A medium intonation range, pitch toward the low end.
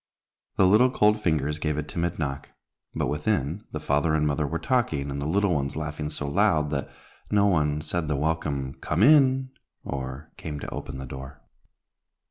Yes: average, 3.4 semitones; very low, 75 Hz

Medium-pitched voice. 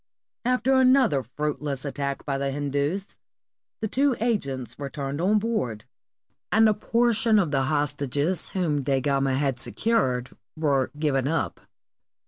Yes: medium, 145 Hz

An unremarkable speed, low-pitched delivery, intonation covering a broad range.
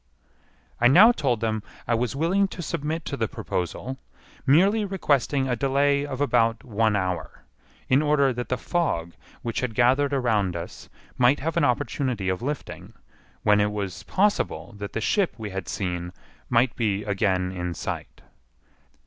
Yes: average, 160 wpm; low, 125 Hz; wide, 5.7 semitones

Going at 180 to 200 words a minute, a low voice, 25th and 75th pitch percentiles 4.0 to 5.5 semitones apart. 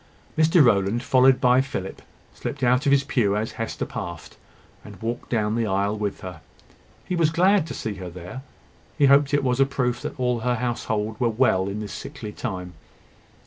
Yes: average, 190 wpm; low, 120 Hz; average, 4.7 semitones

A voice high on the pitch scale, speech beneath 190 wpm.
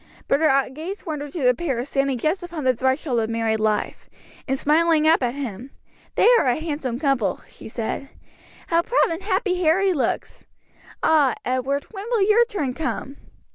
Yes: very high, 285 Hz; average, 175 wpm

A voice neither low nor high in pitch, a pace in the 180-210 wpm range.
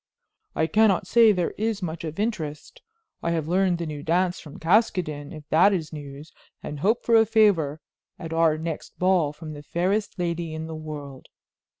Yes: medium, 165 Hz; average, 185 wpm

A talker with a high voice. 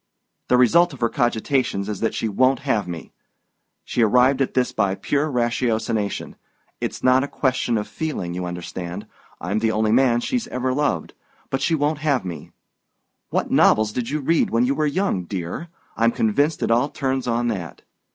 No: low, 120 Hz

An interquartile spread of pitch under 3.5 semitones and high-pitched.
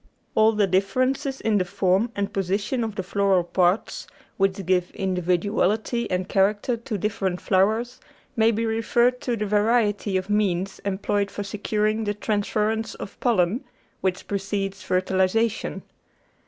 Yes: average, 2.7 semitones; high, 205 Hz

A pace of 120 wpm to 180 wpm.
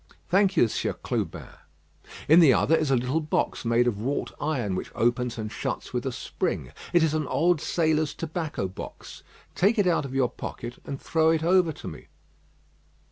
No: average, 190 wpm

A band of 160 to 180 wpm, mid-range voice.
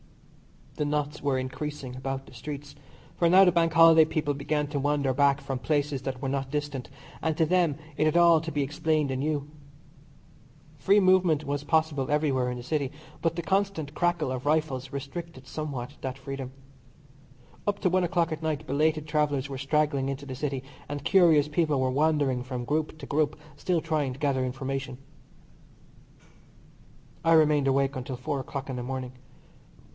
Yes: average, 175 wpm; medium, 145 Hz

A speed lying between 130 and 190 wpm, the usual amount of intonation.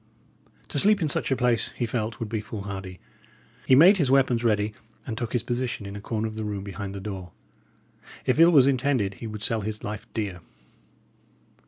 No: average, 200 wpm; average, 3.8 semitones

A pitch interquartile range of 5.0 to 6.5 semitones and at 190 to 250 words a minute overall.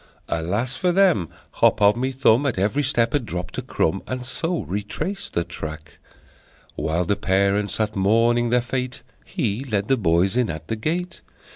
No: wide, 5.4 semitones; average, 175 wpm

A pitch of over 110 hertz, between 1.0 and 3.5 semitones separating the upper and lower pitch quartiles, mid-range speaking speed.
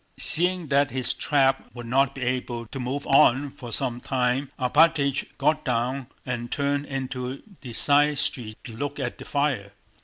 Yes: low, 135 Hz; narrow, 2.4 semitones; average, 165 wpm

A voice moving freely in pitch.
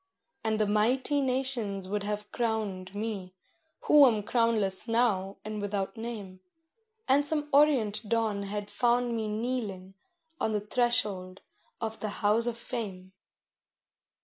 No: average, 3.0 semitones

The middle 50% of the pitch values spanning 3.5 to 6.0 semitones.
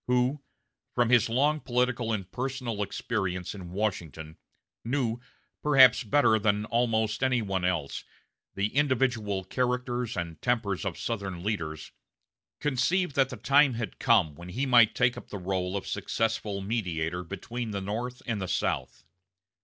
Yes: average, 4.5 semitones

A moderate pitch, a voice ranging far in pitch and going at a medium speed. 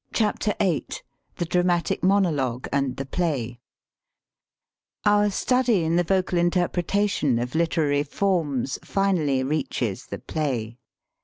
No: medium, 165 Hz; wide, 5.7 semitones; slow, 105 wpm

